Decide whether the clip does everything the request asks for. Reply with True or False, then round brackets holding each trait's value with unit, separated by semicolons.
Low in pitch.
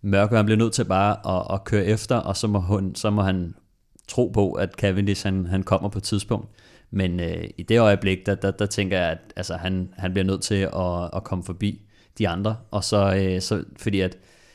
True (100 Hz)